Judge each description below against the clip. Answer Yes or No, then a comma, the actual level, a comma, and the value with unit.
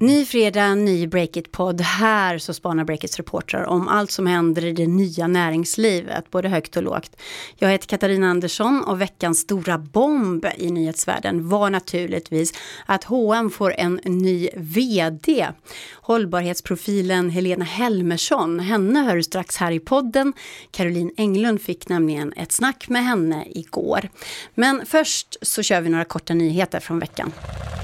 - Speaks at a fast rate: No, average, 145 wpm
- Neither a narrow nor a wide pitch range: Yes, average, 3.9 semitones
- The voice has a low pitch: No, medium, 180 Hz